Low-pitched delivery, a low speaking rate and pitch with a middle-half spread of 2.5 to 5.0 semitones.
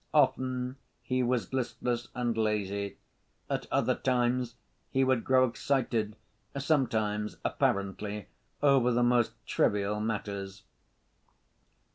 Yes: low, 120 Hz; slow, 100 wpm; average, 3.4 semitones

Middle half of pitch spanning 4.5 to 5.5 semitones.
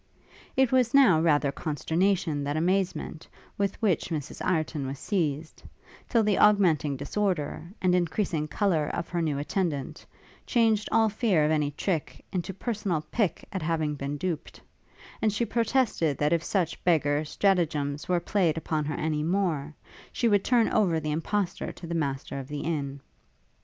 Yes: average, 4.9 semitones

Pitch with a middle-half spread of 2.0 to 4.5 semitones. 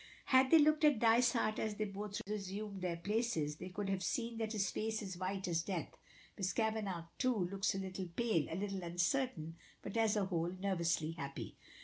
Yes: average, 3.8 semitones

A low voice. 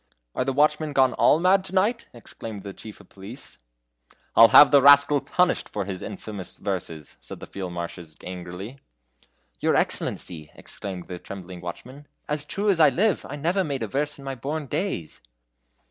Yes: low, 130 Hz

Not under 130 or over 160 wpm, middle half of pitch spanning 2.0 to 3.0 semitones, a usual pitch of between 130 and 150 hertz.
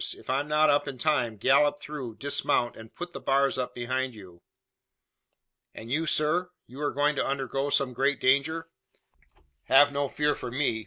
No: average, 175 wpm; average, 2.7 semitones; medium, 140 Hz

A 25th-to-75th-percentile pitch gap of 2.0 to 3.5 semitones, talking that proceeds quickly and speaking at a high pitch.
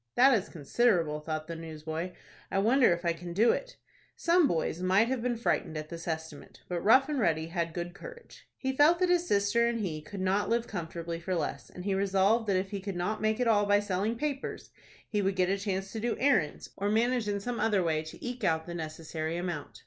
No: wide, 5.5 semitones; fast, 230 wpm; high, 195 Hz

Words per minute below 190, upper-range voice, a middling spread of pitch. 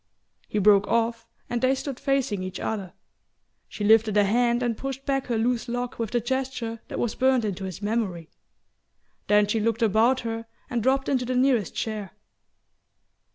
Yes: average, 175 wpm; high, 230 Hz; average, 3.0 semitones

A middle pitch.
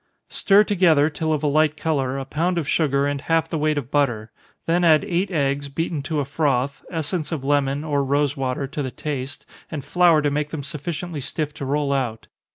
Yes: medium, 145 Hz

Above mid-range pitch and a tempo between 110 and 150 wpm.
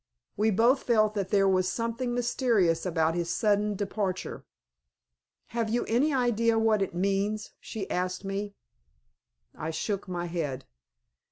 Yes: high, 205 Hz; average, 140 wpm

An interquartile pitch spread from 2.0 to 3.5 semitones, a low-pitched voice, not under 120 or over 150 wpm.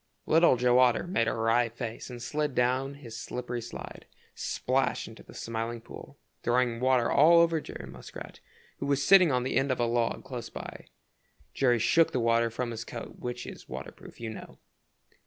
No: narrow, 2.5 semitones; low, 125 Hz; average, 190 wpm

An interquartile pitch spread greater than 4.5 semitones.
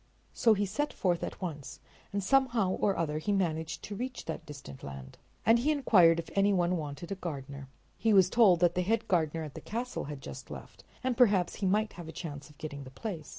Yes: wide, 5.4 semitones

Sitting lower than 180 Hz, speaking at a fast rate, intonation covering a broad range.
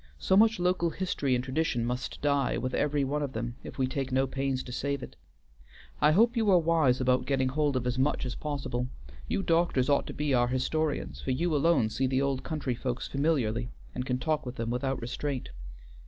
No: low, 135 Hz; fast, 215 wpm; average, 3.2 semitones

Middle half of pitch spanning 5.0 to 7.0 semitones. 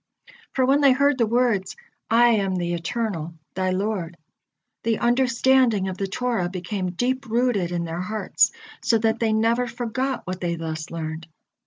Yes: average, 5.3 semitones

